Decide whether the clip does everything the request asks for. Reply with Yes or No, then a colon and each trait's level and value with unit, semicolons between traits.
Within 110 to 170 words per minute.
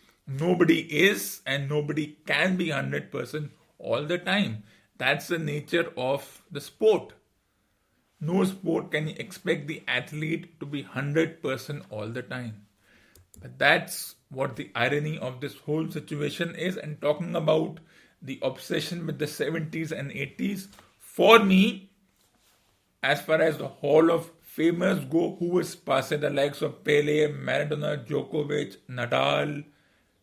Yes: slow, 135 wpm